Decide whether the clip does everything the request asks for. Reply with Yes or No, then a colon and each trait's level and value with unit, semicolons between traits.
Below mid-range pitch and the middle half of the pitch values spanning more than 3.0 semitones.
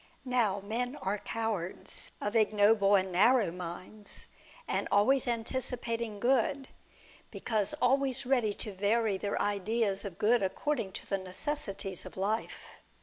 No: high, 215 Hz; average, 3.6 semitones